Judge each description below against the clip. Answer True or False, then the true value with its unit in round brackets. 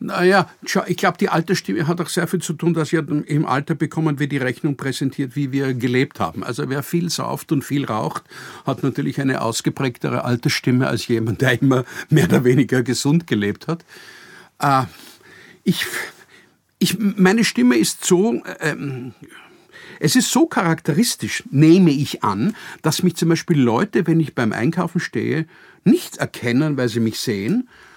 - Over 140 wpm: True (165 wpm)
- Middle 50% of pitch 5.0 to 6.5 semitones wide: True (5.3 semitones)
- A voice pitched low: False (155 Hz)